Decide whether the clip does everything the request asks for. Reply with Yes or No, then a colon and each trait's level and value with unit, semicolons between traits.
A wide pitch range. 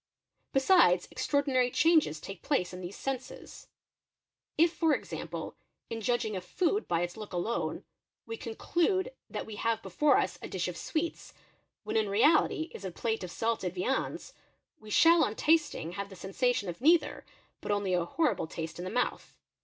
Yes: wide, 8.2 semitones